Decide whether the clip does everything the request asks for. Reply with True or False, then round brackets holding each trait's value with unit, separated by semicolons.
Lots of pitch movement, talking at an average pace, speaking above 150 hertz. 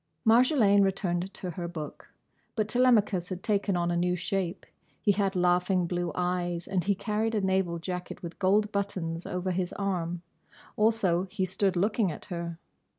False (2.5 semitones; 165 wpm; 185 Hz)